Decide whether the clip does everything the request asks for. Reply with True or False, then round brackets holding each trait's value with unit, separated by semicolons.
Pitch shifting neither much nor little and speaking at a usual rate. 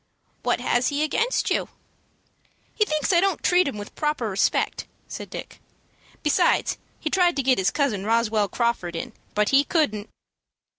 False (6.6 semitones; 160 wpm)